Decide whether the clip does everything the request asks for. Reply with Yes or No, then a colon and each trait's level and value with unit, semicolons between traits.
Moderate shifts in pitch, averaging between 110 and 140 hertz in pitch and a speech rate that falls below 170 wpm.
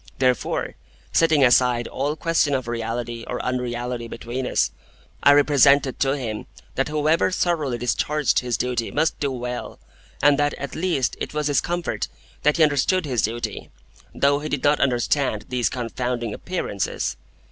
Yes: average, 3.4 semitones; low, 135 Hz; average, 155 wpm